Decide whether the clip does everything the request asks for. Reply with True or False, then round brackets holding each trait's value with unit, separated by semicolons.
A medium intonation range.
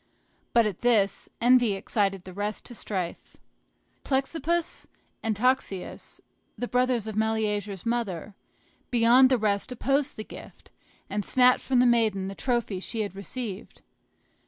True (3.8 semitones)